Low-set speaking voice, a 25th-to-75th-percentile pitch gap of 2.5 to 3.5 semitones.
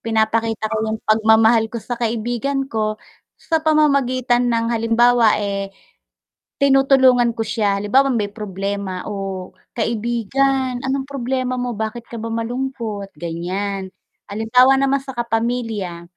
No: high, 230 Hz; average, 3.1 semitones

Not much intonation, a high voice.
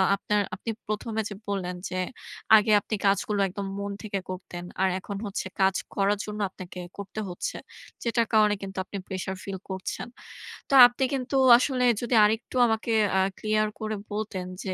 Yes: narrow, 2.2 semitones; high, 205 Hz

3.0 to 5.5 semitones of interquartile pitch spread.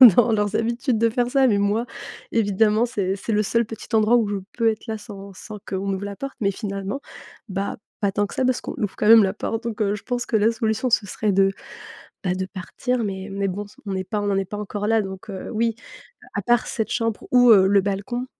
No: narrow, 2.5 semitones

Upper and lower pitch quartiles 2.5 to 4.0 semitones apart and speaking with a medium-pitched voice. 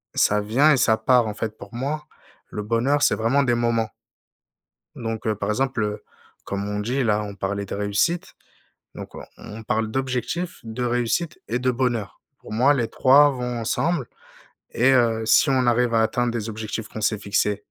No: average, 3.2 semitones; low, 115 Hz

